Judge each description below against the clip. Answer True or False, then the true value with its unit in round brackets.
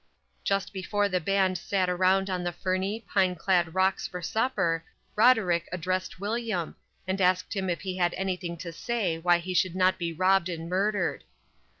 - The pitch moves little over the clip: True (1.8 semitones)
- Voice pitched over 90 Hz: True (185 Hz)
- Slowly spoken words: False (175 wpm)